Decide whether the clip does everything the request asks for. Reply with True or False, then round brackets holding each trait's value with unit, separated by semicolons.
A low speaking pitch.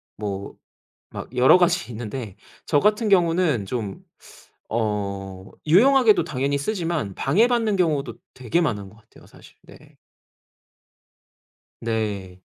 True (130 Hz)